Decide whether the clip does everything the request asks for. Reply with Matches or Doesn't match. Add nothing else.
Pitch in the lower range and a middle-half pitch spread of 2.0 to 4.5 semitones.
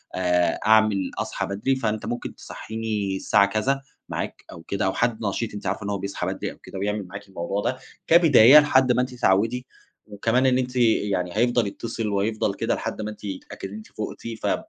Matches